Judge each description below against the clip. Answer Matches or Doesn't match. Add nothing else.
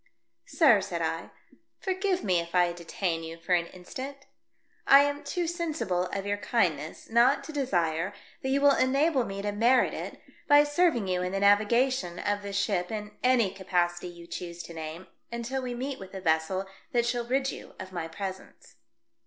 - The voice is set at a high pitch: Matches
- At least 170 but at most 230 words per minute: Matches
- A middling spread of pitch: Doesn't match